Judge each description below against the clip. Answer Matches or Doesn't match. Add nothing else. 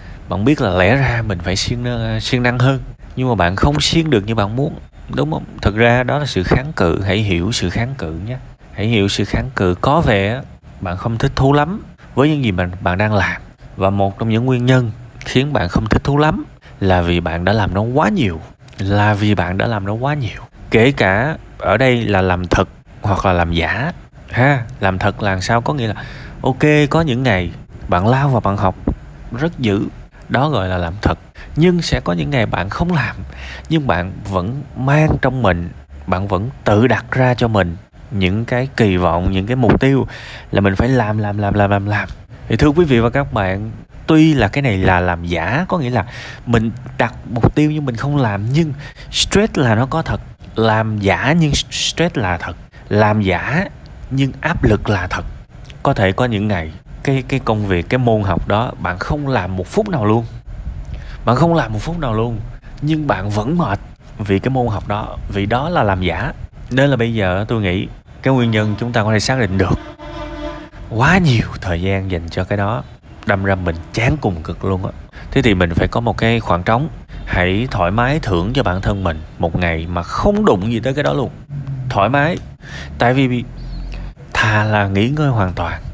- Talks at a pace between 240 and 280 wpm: Doesn't match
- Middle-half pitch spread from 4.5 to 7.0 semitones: Matches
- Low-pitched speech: Matches